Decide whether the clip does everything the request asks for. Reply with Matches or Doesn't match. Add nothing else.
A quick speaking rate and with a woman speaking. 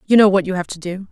Matches